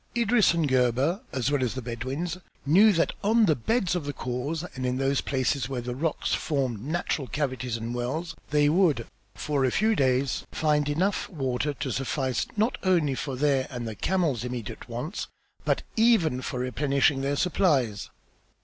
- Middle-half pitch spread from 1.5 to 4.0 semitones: No, average, 4.7 semitones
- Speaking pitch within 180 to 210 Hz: No, medium, 140 Hz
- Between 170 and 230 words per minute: Yes, average, 175 wpm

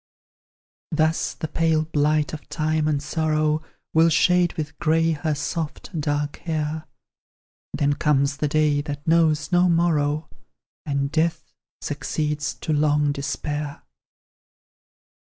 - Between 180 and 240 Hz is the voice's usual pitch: No, medium, 155 Hz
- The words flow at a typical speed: No, slow, 115 wpm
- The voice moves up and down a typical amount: No, narrow, 1.5 semitones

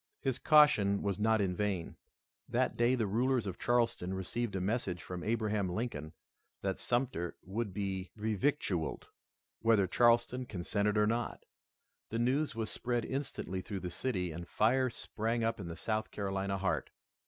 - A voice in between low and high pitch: No, low, 105 Hz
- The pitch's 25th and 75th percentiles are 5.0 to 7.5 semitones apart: No, average, 3.8 semitones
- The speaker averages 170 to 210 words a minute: No, average, 155 wpm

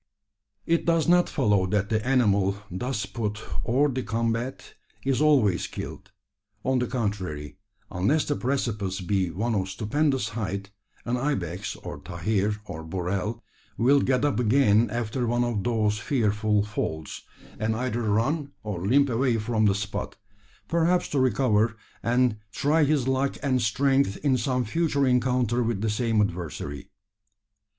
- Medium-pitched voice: No, low, 115 Hz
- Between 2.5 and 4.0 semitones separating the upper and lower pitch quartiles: No, average, 4.4 semitones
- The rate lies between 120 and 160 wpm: Yes, average, 145 wpm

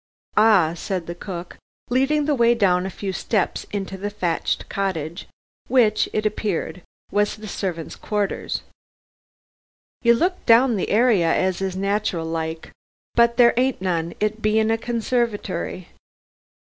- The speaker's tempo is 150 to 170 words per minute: No, average, 140 wpm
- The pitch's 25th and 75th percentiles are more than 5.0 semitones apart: No, average, 4.3 semitones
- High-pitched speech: Yes, high, 205 Hz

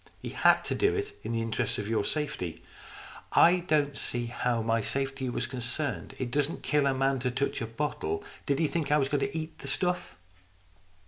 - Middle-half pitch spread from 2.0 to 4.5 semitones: Yes, average, 4.2 semitones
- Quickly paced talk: Yes, fast, 210 wpm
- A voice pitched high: No, low, 135 Hz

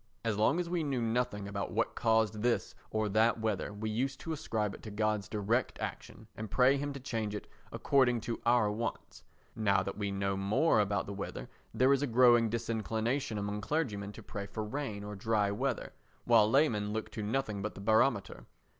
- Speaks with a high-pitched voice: No, low, 110 Hz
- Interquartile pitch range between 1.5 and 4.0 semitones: Yes, average, 3.1 semitones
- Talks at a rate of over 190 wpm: Yes, average, 200 wpm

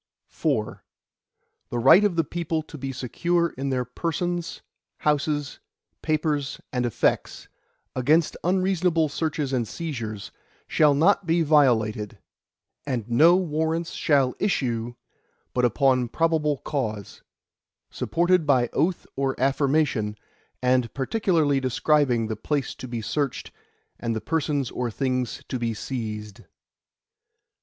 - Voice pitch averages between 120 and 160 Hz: Yes, medium, 140 Hz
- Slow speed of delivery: Yes, slow, 120 wpm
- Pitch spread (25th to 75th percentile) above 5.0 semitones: No, average, 4.6 semitones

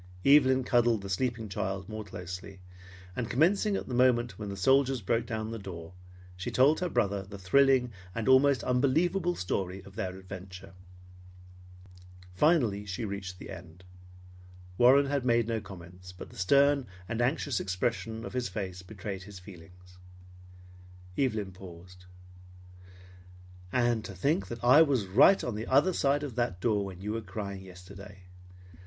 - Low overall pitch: Yes, low, 110 Hz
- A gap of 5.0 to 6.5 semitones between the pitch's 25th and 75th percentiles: Yes, wide, 5.4 semitones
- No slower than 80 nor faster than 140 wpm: No, average, 155 wpm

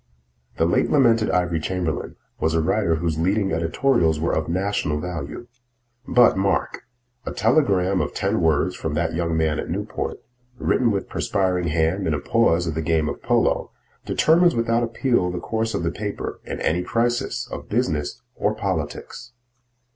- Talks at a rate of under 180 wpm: Yes, average, 165 wpm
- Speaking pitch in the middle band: No, very low, 90 Hz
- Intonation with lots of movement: Yes, wide, 5.7 semitones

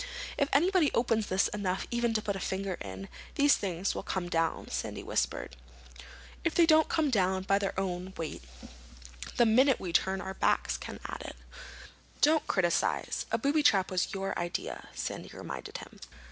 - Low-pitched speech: No, high, 195 Hz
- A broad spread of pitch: Yes, wide, 6.8 semitones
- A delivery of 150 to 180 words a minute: Yes, average, 170 wpm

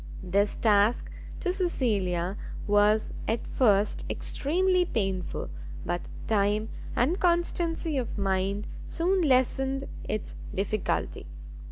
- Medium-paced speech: No, slow, 95 wpm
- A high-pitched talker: Yes, high, 220 Hz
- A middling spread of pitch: No, wide, 8.0 semitones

